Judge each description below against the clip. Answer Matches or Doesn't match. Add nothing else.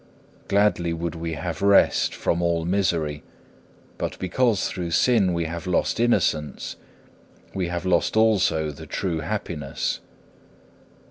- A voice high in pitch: Doesn't match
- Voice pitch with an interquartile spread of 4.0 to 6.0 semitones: Doesn't match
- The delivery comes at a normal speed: Doesn't match